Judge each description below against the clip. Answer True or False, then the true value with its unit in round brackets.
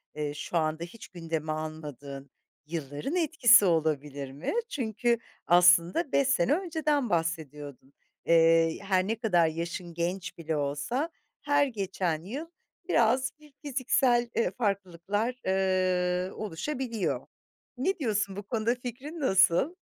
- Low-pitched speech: False (185 Hz)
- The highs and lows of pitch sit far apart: True (7.0 semitones)